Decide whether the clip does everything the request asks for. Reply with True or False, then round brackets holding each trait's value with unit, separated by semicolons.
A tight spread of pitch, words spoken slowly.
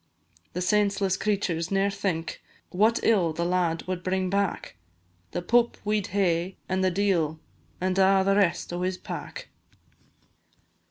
False (2.2 semitones; 155 wpm)